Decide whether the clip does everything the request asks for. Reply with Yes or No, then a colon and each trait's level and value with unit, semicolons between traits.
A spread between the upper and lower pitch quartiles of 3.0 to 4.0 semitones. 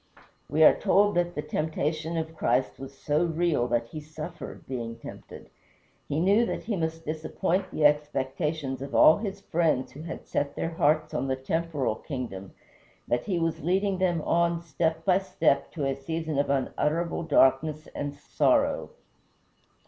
Yes: average, 3.4 semitones